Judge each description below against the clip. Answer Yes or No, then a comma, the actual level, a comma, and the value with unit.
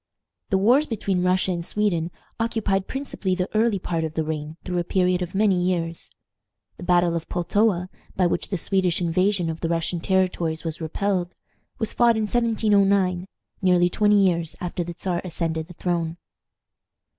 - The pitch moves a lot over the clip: No, average, 2.8 semitones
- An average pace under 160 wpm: No, average, 170 wpm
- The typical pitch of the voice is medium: Yes, medium, 180 Hz